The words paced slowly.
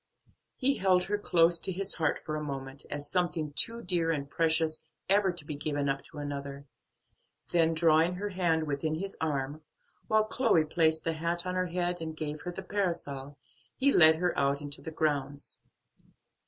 No: average, 180 wpm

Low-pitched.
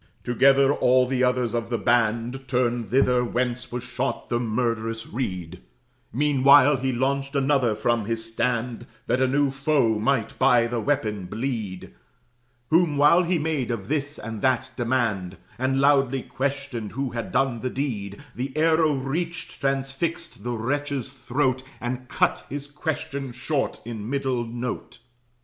Yes: low, 130 Hz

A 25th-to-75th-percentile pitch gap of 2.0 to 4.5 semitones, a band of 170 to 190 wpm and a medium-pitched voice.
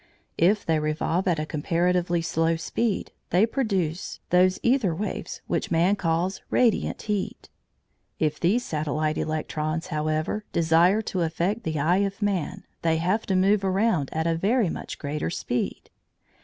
No: average, 3.7 semitones; average, 150 wpm; medium, 175 Hz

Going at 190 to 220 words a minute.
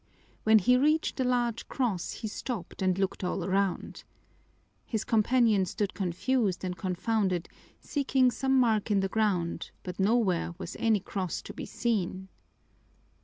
No: average, 145 wpm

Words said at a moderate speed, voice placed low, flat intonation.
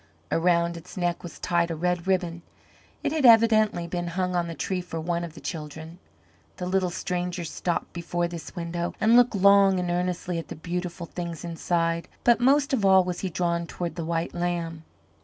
No: average, 195 wpm; medium, 175 Hz; narrow, 1.5 semitones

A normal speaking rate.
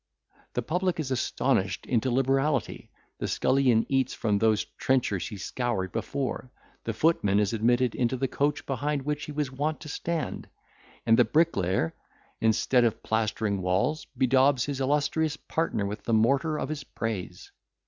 Yes: average, 145 wpm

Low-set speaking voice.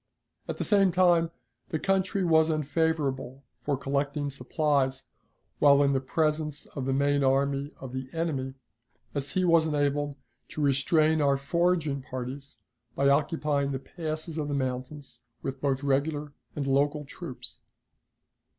No: medium, 145 Hz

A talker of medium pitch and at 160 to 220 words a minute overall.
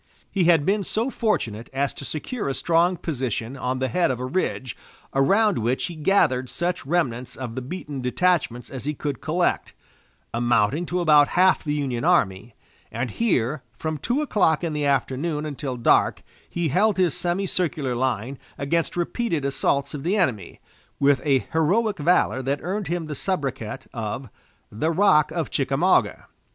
Yes: medium, 150 Hz; average, 165 wpm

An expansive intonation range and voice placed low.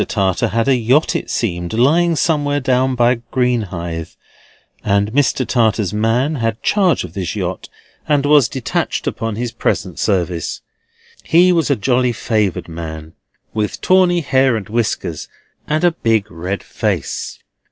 Yes: wide, 5.8 semitones; low, 115 Hz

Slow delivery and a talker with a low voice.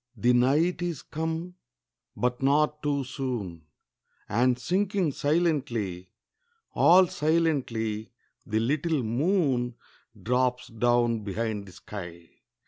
Yes: slow, 100 wpm; low, 125 Hz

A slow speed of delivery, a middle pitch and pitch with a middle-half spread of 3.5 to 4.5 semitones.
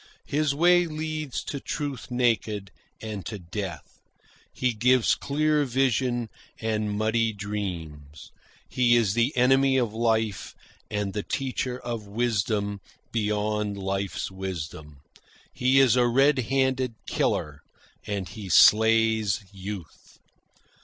No: slow, 115 wpm; low, 110 Hz; average, 4.0 semitones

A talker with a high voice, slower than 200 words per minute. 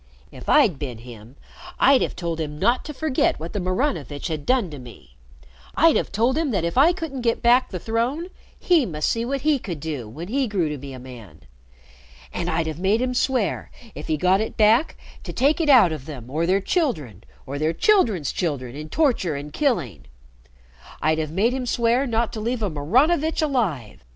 No: high, 195 Hz; fast, 205 wpm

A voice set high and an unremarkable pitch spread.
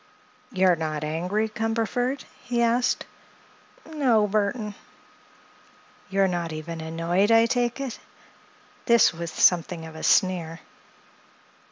No: high, 195 Hz; wide, 5.7 semitones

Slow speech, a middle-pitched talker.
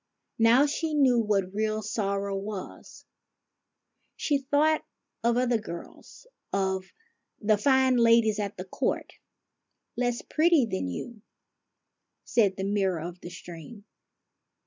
No: slow, 125 wpm; high, 215 Hz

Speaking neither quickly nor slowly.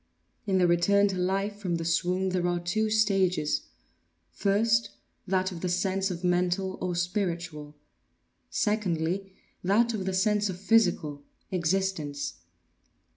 No: slow, 130 wpm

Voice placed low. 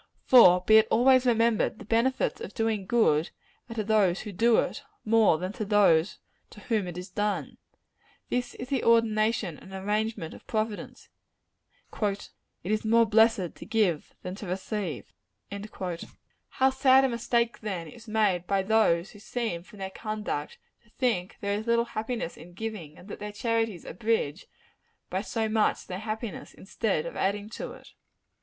No: high, 215 Hz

